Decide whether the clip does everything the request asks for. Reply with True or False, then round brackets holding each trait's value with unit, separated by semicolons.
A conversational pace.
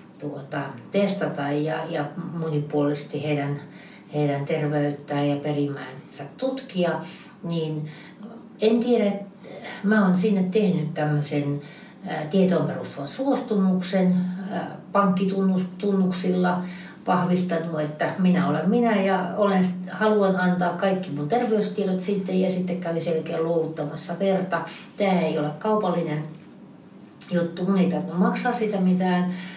True (110 wpm)